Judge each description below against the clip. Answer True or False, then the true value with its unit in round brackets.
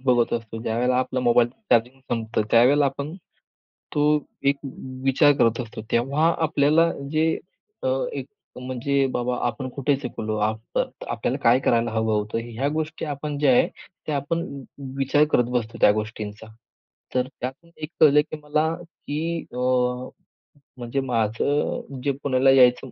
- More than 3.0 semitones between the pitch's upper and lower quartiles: True (3.8 semitones)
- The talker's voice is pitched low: True (130 Hz)